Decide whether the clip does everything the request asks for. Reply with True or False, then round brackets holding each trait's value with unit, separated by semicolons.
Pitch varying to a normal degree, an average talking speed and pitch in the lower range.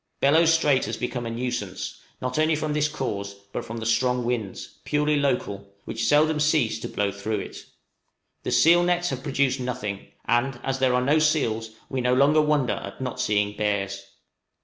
True (5.0 semitones; 185 wpm; 125 Hz)